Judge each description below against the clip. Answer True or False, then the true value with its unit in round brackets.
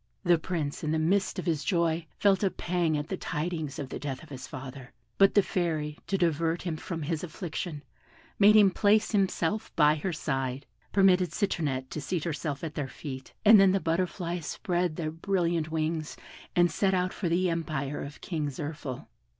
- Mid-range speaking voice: True (165 Hz)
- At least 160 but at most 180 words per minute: False (190 wpm)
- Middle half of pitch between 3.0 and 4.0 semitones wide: True (3.4 semitones)